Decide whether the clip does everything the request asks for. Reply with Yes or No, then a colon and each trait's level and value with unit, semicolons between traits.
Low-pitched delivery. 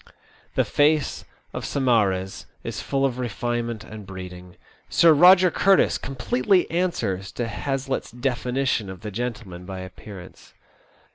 Yes: low, 120 Hz